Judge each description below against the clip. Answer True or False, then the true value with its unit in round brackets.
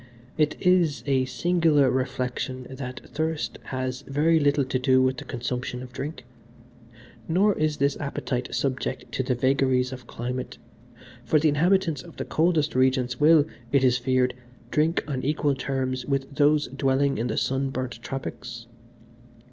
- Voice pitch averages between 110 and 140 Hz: True (135 Hz)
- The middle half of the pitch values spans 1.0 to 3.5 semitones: True (2.7 semitones)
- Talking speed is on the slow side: False (155 wpm)